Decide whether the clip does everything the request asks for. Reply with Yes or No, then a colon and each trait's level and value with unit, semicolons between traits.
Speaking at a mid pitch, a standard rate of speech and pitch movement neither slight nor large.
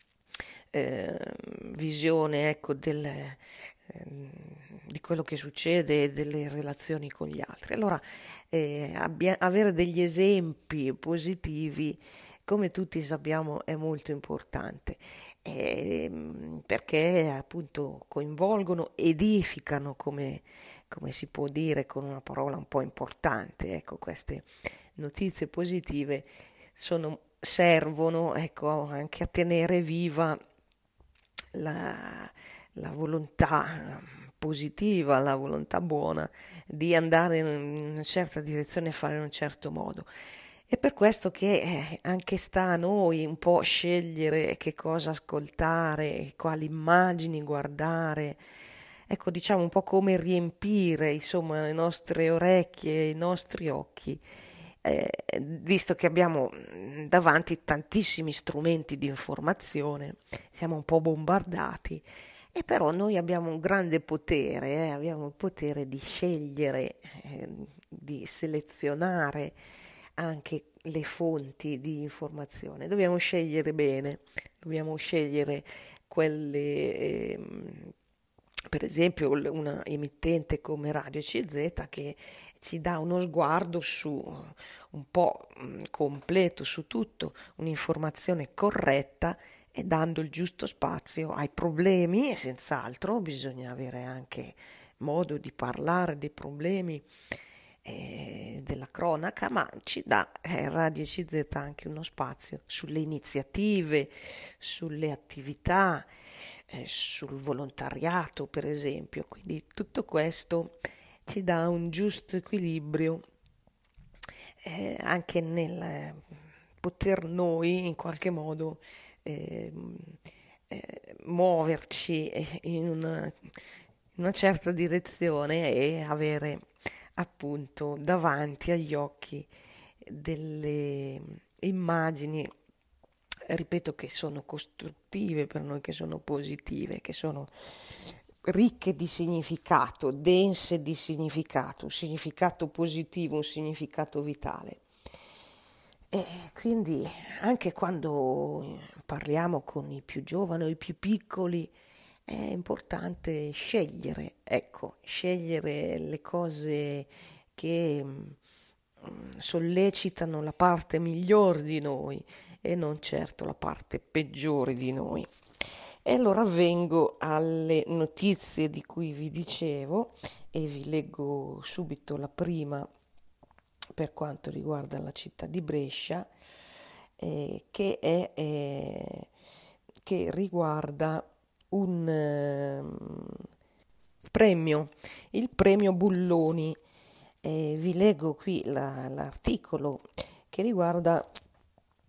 No: medium, 160 Hz; slow, 105 wpm; average, 3.0 semitones